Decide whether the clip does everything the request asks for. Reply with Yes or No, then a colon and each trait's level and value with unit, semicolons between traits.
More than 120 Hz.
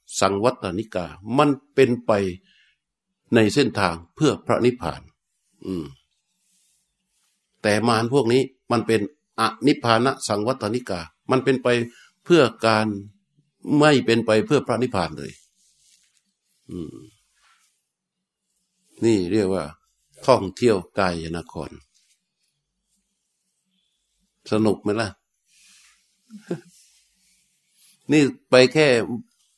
Yes: low, 130 Hz